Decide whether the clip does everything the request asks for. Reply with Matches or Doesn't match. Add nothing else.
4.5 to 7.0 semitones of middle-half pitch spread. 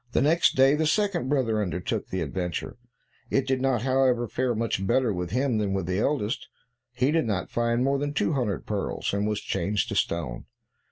Matches